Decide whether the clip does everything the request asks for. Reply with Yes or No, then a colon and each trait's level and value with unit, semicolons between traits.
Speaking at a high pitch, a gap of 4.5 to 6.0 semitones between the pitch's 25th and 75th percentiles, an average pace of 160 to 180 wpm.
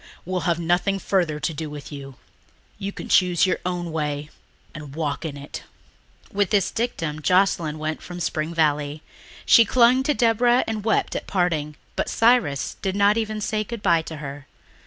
No: medium, 175 Hz; average, 5.2 semitones; average, 175 wpm